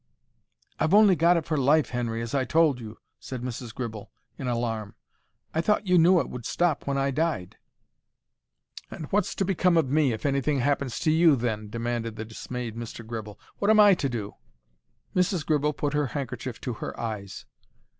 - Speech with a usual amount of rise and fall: No, wide, 5.7 semitones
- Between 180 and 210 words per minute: Yes, average, 185 wpm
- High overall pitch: No, low, 135 Hz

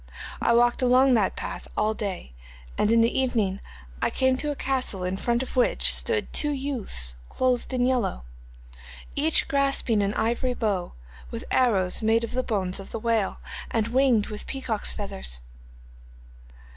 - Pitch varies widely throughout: No, average, 4.0 semitones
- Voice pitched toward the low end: No, high, 230 Hz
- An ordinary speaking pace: Yes, average, 165 wpm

